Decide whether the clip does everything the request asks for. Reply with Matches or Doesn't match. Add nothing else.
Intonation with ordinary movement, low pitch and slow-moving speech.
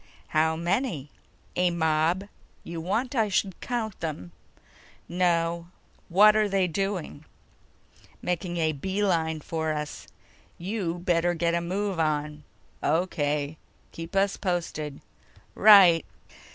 Doesn't match